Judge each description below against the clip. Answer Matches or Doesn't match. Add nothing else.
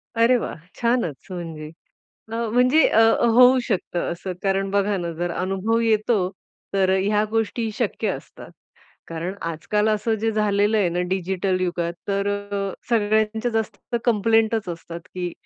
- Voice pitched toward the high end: Matches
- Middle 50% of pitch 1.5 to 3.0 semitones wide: Doesn't match